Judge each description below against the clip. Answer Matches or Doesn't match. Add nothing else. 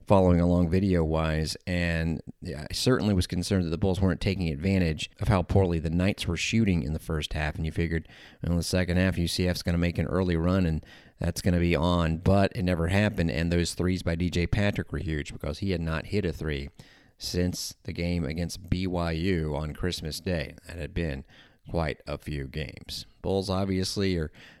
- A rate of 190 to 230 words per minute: Matches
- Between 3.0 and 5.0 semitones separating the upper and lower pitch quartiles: Doesn't match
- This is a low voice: Matches